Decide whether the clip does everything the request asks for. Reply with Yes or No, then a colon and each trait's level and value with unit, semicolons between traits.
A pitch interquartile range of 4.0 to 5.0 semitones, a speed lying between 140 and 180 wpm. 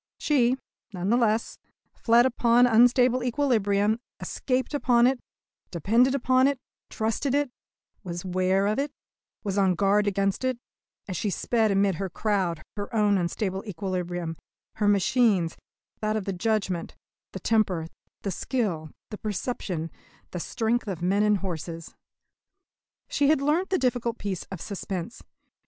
Yes: average, 4.6 semitones; average, 145 wpm